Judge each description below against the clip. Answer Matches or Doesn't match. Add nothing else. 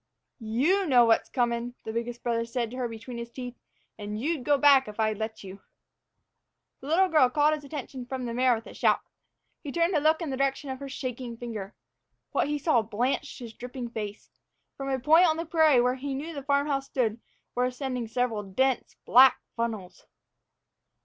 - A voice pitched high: Matches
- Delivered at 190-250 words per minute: Matches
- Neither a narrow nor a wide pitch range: Matches